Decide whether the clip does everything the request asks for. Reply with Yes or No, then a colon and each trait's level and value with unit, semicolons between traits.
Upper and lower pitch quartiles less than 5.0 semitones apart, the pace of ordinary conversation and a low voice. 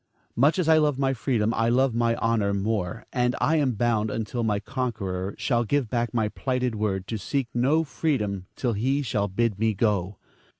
Yes: average, 3.7 semitones; average, 195 wpm; low, 115 Hz